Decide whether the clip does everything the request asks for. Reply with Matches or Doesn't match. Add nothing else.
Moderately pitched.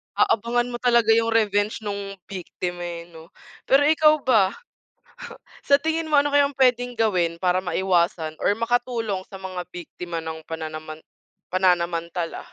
Doesn't match